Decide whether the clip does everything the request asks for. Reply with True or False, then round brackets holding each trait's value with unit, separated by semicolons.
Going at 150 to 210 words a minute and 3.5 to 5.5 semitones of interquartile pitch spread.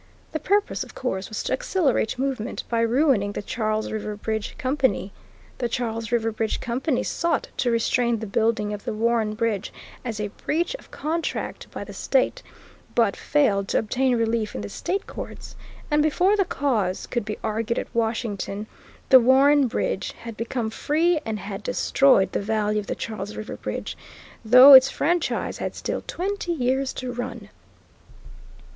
True (165 wpm; 4.0 semitones)